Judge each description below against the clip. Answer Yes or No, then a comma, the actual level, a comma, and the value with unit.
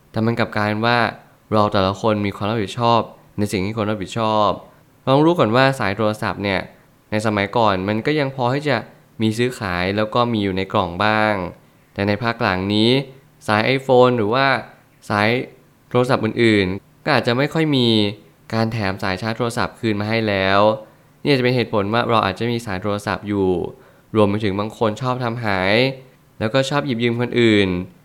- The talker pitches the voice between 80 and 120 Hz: Yes, low, 110 Hz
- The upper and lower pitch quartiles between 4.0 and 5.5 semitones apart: No, average, 3.3 semitones